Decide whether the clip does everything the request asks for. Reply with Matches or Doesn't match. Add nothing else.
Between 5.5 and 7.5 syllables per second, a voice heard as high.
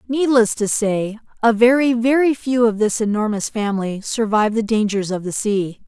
Doesn't match